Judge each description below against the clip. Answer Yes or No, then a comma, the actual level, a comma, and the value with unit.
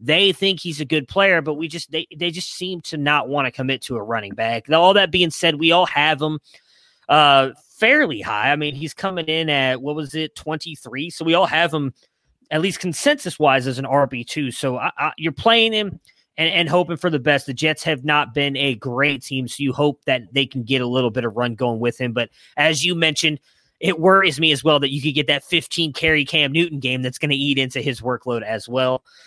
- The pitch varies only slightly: No, average, 3.7 semitones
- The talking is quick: Yes, fast, 240 wpm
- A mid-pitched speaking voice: Yes, medium, 150 Hz